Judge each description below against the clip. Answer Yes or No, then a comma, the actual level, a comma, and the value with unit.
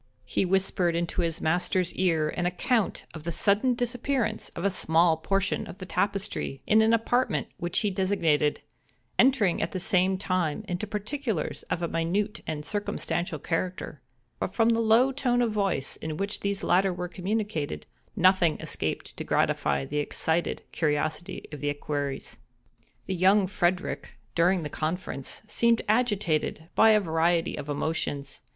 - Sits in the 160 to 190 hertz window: Yes, medium, 185 Hz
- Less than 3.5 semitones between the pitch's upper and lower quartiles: No, average, 4.4 semitones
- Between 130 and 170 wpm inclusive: Yes, average, 155 wpm